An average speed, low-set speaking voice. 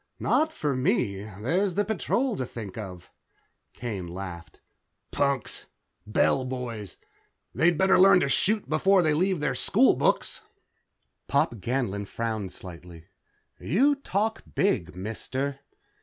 No: slow, 125 wpm; low, 130 Hz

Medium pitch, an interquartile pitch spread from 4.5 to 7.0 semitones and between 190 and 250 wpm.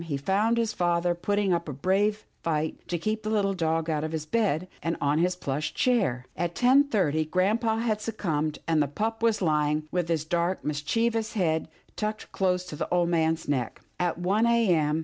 Yes: medium, 175 Hz; average, 5.2 semitones; average, 200 wpm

